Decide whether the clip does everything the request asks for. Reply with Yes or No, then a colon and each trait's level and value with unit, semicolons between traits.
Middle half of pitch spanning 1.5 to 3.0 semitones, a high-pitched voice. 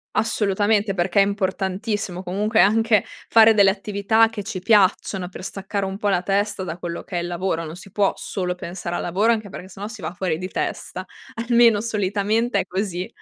Yes: narrow, 2.6 semitones; high, 195 Hz